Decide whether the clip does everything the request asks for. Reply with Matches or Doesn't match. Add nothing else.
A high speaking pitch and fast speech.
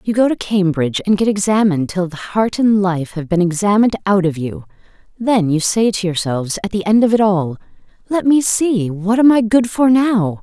Matches